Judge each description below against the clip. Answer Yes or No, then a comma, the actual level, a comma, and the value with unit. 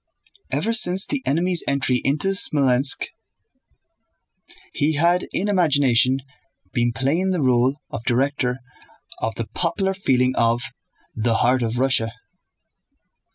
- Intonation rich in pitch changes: Yes, wide, 5.9 semitones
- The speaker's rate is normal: No, slow, 115 wpm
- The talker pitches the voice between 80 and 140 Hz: Yes, low, 135 Hz